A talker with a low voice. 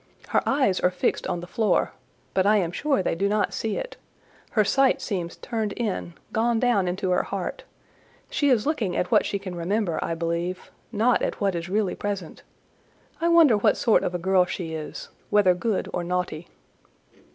No: high, 195 Hz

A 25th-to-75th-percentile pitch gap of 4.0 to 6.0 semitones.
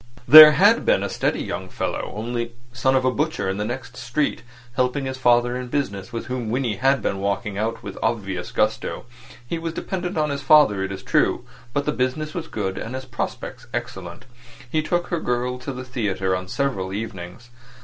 Yes: average, 5.1 semitones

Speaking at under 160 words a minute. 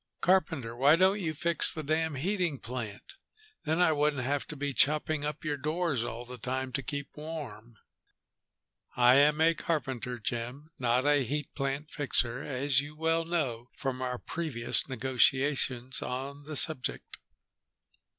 Yes: average, 150 wpm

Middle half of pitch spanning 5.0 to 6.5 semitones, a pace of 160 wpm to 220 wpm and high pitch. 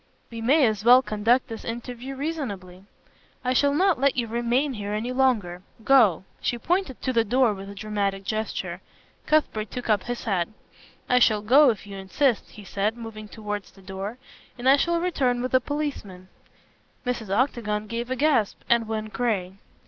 No: average, 3.8 semitones; average, 180 wpm; high, 230 Hz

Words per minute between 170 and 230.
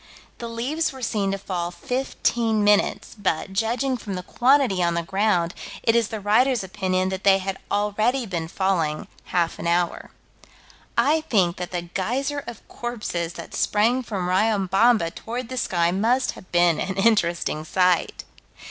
No: average, 160 wpm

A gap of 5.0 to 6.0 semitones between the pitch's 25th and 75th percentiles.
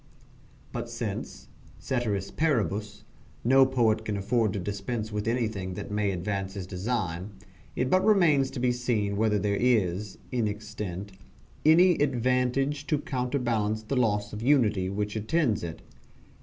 No: average, 3.7 semitones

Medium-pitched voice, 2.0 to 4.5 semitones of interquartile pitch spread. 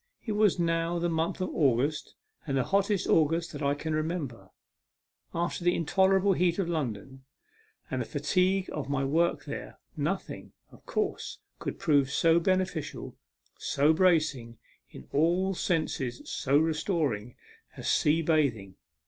Yes: medium, 160 Hz; average, 4.0 semitones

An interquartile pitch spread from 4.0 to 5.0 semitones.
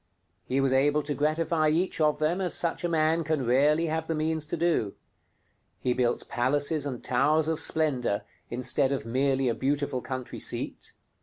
No: average, 3.4 semitones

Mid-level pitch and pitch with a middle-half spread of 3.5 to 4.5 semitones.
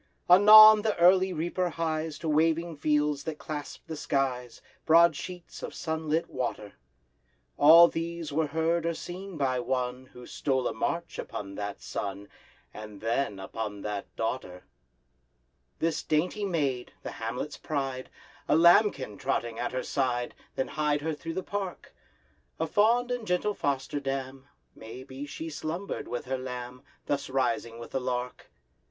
No: medium, 145 Hz; average, 5.0 semitones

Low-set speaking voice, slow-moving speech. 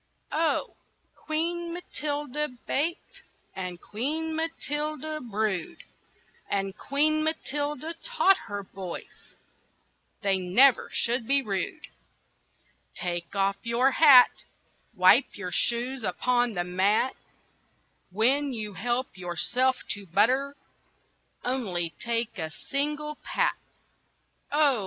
No: very high, 250 Hz; slow, 100 wpm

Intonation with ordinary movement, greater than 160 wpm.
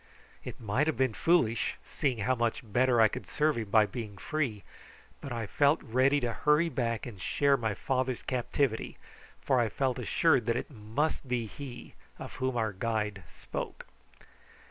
Yes: average, 3.7 semitones; average, 170 wpm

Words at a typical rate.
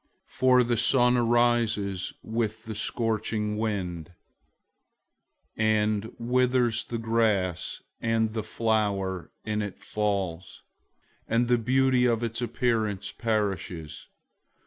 No: slow, 105 wpm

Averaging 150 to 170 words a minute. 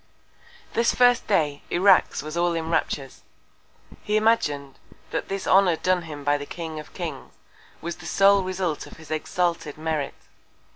Yes: average, 155 wpm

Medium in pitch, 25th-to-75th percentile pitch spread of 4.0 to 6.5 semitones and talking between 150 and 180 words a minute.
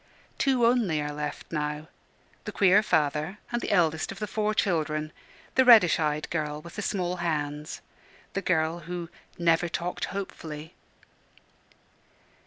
No: medium, 170 Hz; average, 4.4 semitones; average, 140 wpm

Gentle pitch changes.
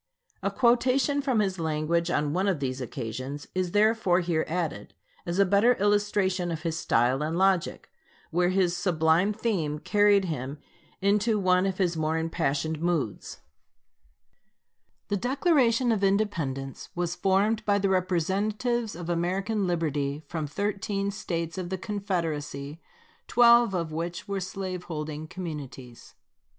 No: average, 4.3 semitones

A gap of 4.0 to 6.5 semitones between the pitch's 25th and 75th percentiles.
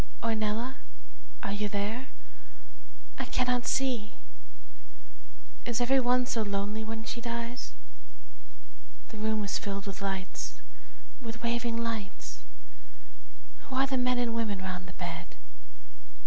No: average, 3.1 semitones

